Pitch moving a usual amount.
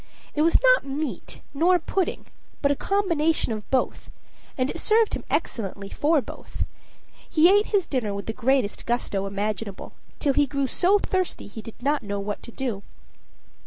No: wide, 7.8 semitones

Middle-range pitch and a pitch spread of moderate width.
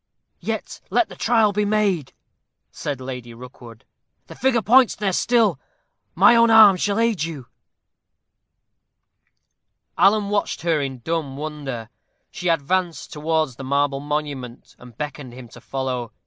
No: medium, 150 Hz; wide, 7.5 semitones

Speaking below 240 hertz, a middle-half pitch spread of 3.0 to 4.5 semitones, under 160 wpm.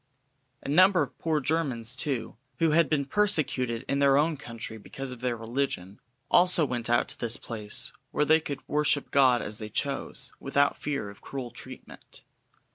No: low, 135 Hz; average, 4.2 semitones; average, 175 wpm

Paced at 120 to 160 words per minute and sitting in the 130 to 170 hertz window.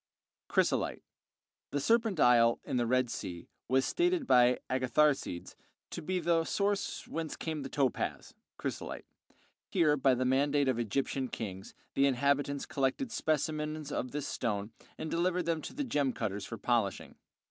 Yes: average, 155 wpm; medium, 140 Hz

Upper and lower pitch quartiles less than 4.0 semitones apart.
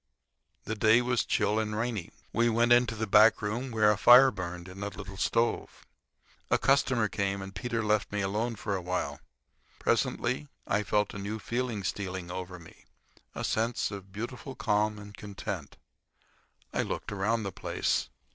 Yes: average, 3.0 semitones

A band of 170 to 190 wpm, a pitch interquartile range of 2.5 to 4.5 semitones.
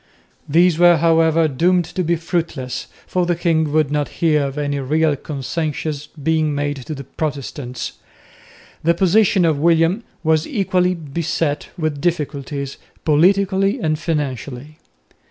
No: slow, 135 wpm; average, 2.9 semitones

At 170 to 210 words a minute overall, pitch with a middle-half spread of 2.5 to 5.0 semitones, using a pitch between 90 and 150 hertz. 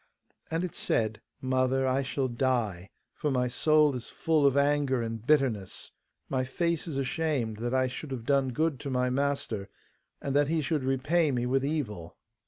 Yes: average, 180 wpm; average, 2.8 semitones; low, 135 Hz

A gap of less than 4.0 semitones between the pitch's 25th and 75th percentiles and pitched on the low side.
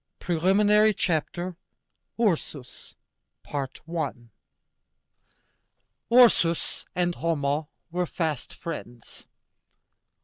No: average, 3.4 semitones; medium, 170 Hz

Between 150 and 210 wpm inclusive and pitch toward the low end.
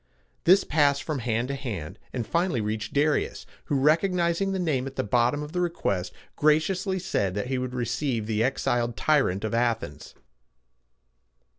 Yes: average, 160 wpm; low, 130 Hz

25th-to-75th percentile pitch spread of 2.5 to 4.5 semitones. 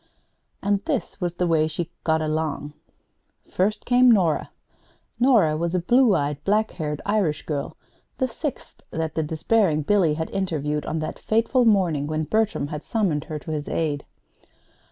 No: average, 5.3 semitones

